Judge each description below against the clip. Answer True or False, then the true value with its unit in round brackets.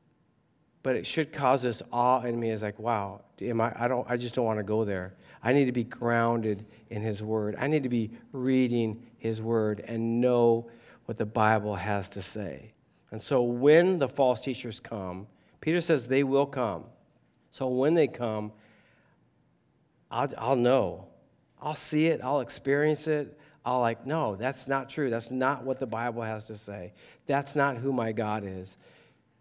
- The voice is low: True (120 Hz)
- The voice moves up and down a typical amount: True (3.7 semitones)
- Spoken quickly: False (185 wpm)